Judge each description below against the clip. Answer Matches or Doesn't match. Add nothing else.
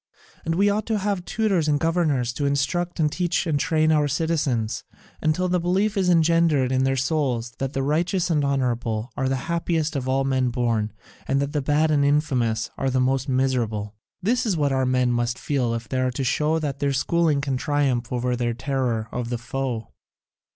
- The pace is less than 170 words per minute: Doesn't match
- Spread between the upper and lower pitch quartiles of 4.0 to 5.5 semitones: Matches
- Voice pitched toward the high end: Doesn't match